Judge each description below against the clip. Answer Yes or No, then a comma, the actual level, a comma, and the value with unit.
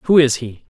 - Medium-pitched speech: No, low, 130 Hz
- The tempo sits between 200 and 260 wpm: Yes, fast, 230 wpm